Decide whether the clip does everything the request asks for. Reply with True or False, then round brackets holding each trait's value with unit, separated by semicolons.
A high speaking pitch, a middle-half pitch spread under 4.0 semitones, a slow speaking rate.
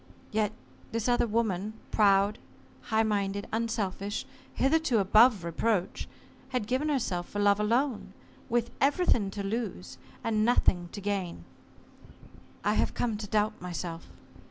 True (215 Hz; 2.9 semitones; 130 wpm)